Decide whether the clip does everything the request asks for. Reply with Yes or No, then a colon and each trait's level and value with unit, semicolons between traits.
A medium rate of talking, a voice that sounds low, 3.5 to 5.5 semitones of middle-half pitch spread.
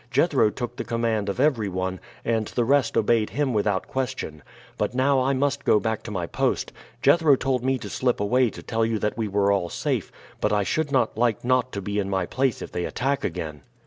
No: fast, 220 wpm; low, 115 Hz; average, 4.3 semitones